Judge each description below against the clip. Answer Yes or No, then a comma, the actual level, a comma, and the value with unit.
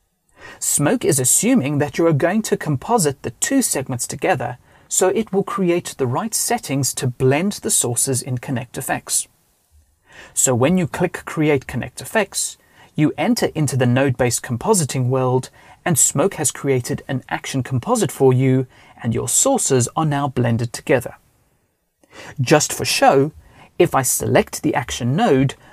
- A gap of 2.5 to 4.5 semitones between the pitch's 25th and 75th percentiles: No, average, 5.2 semitones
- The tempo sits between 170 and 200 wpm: No, average, 150 wpm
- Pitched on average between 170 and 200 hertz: No, low, 135 Hz